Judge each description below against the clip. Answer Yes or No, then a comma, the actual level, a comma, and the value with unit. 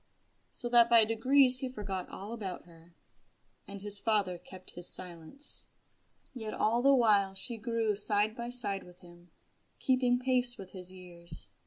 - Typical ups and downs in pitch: Yes, average, 4.6 semitones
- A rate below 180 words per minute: Yes, average, 155 wpm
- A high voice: Yes, high, 210 Hz